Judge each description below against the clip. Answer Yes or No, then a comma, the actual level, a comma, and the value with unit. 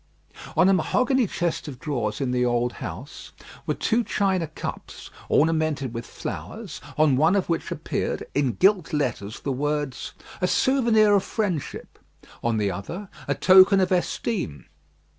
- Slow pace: No, average, 150 wpm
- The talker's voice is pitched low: No, medium, 155 Hz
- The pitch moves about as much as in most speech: No, wide, 7.1 semitones